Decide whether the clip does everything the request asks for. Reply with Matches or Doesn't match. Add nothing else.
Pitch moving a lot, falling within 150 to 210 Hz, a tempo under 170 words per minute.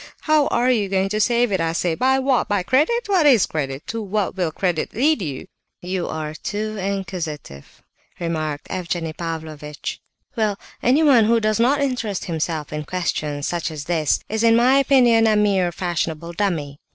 Doesn't match